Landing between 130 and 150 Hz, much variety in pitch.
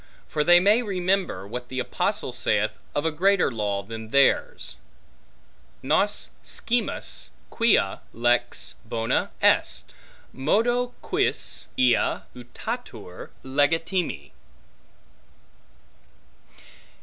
Yes: medium, 140 Hz; wide, 8.8 semitones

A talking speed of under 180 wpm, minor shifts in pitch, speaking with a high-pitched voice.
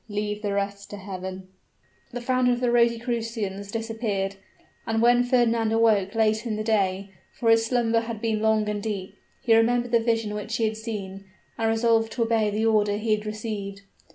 No: average, 185 wpm; narrow, 1.9 semitones; high, 220 Hz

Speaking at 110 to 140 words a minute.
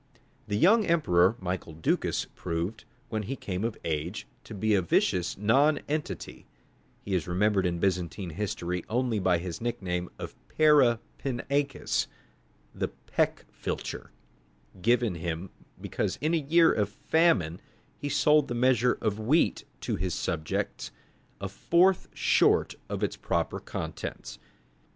Yes: slow, 135 wpm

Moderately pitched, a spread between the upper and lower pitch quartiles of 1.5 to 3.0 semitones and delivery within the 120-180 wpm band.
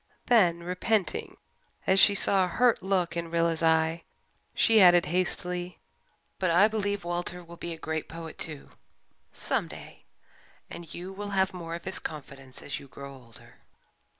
Yes: medium, 175 Hz; narrow, 2.6 semitones; average, 160 wpm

